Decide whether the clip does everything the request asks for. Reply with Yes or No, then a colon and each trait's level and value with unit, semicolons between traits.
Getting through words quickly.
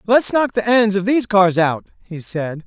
Yes: fast, 225 wpm